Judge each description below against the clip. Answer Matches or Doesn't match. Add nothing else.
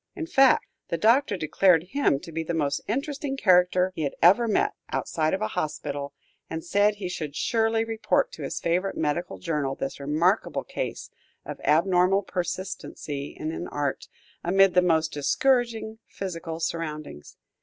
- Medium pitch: Matches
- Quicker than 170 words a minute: Doesn't match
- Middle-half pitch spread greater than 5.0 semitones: Matches